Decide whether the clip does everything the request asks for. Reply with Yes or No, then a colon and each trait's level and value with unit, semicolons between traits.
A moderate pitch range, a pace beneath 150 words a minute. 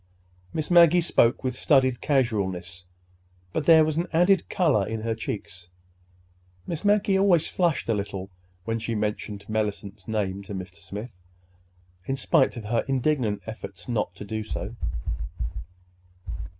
No: wide, 7.1 semitones; slow, 135 wpm